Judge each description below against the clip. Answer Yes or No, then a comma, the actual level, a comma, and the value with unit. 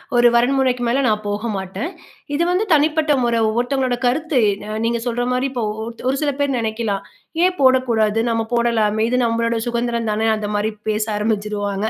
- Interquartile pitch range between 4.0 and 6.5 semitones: No, average, 3.0 semitones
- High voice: Yes, high, 235 Hz